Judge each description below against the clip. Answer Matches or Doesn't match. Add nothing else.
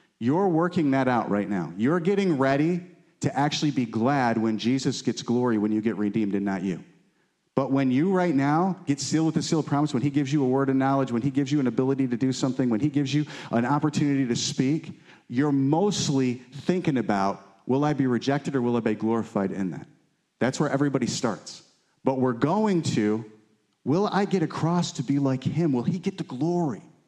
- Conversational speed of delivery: Doesn't match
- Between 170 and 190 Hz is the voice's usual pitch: Doesn't match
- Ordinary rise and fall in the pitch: Matches